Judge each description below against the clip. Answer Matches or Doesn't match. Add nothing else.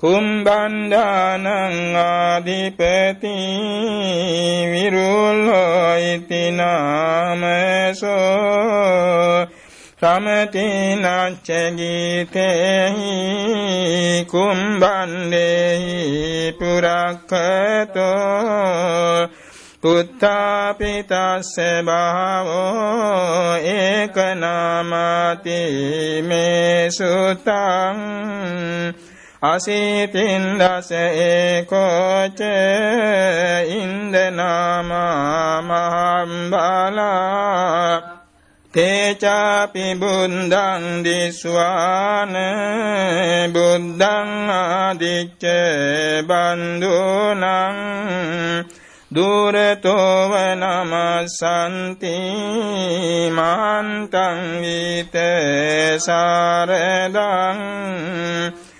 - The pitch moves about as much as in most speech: Doesn't match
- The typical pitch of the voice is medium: Matches